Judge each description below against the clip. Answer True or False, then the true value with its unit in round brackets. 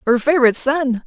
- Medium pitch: False (265 Hz)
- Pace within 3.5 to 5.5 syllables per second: False (6.5 syllables/s)